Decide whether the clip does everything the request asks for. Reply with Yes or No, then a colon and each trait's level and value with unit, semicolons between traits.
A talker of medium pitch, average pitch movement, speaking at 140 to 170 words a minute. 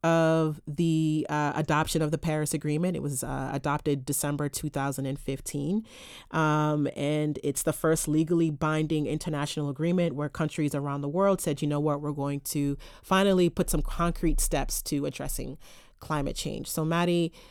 No: medium, 155 Hz; narrow, 2.1 semitones; average, 160 wpm